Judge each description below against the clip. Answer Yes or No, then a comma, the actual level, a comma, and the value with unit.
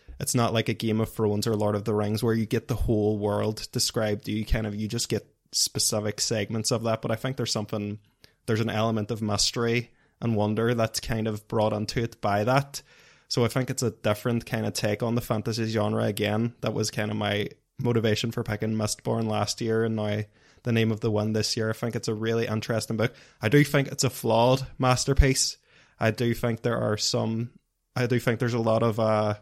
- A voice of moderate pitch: No, low, 110 Hz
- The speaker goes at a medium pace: No, fast, 225 wpm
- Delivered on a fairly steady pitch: Yes, narrow, 1.9 semitones